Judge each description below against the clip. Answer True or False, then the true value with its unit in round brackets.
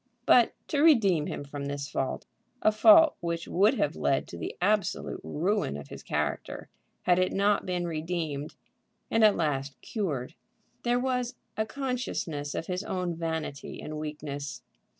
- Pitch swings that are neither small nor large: False (6.7 semitones)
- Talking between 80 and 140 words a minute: False (155 wpm)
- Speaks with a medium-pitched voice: True (170 Hz)